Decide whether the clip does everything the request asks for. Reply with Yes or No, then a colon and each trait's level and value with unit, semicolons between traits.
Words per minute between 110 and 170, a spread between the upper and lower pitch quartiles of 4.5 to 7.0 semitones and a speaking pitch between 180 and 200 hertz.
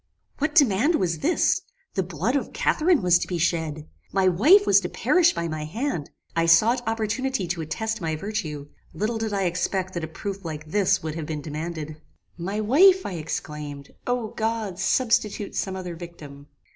No: average, 180 wpm; wide, 5.6 semitones; medium, 185 Hz